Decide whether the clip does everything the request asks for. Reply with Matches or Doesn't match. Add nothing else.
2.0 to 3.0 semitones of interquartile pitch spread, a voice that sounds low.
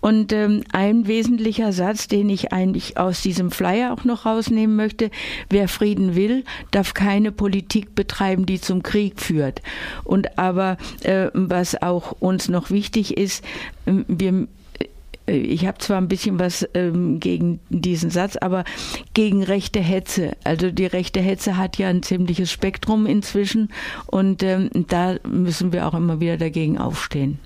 Doesn't match